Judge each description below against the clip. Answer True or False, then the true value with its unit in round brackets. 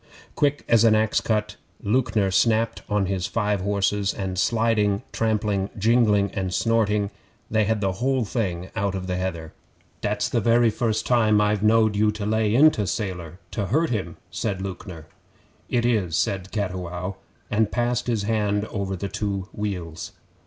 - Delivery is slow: False (160 wpm)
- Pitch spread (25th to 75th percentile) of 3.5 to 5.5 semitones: False (2.6 semitones)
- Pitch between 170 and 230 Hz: False (105 Hz)